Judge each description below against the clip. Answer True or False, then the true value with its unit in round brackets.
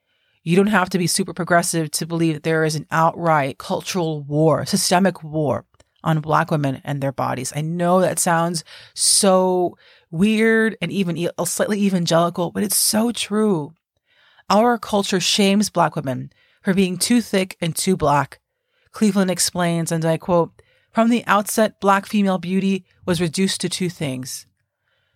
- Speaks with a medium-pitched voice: True (175 Hz)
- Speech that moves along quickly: False (155 wpm)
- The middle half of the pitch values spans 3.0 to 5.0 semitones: True (3.4 semitones)